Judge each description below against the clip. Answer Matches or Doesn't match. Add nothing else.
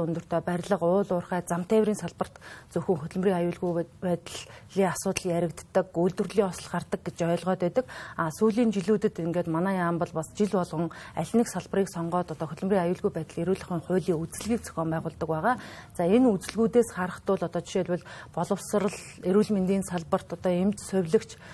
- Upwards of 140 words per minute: Matches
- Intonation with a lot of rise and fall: Doesn't match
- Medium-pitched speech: Matches